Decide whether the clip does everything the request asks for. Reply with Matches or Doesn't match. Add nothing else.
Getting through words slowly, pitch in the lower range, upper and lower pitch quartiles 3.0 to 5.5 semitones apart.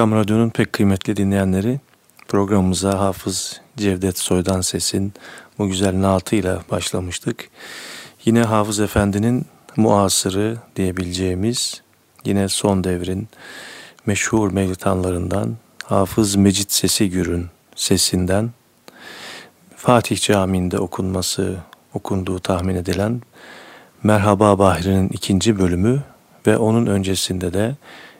Doesn't match